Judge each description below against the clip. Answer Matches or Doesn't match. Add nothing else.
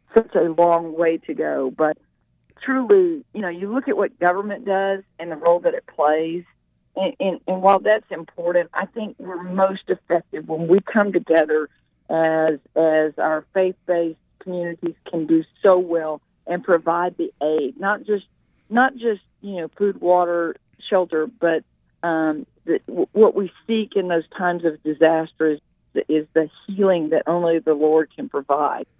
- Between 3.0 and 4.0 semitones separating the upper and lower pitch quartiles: Matches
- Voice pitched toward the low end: Doesn't match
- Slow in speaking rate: Doesn't match